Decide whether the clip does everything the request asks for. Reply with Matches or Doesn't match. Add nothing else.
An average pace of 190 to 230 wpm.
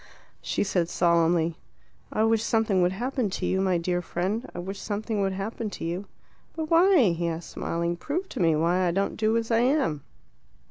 Matches